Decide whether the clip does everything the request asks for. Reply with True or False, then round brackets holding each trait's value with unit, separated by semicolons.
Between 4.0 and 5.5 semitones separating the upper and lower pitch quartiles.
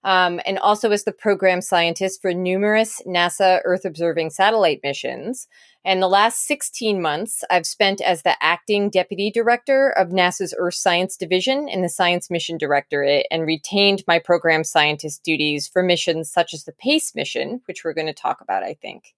False (3.2 semitones)